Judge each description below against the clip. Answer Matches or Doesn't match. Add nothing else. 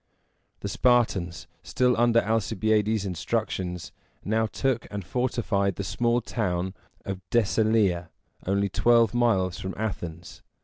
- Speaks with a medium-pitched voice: Doesn't match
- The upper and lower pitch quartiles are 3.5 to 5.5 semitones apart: Matches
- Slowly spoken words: Matches